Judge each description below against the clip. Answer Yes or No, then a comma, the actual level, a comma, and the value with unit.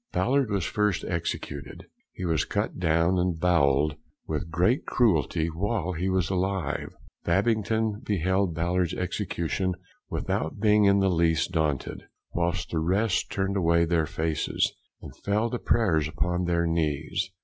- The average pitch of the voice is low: Yes, very low, 90 Hz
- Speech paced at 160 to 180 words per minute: No, average, 140 wpm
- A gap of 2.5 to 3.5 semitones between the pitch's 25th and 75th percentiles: Yes, average, 3.2 semitones